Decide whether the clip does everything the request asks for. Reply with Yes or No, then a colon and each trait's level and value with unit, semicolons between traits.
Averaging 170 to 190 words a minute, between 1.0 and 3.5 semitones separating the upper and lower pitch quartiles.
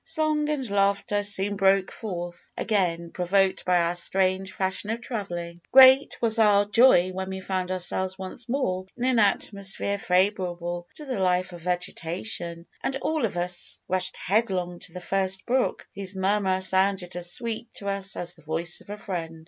Yes: average, 175 wpm; average, 2.7 semitones